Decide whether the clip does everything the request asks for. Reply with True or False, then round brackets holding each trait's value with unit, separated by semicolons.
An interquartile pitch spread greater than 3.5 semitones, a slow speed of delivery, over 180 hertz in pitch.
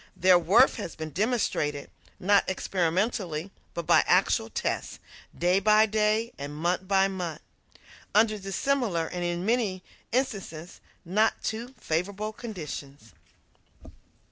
True (4.0 semitones; 115 wpm; 190 Hz)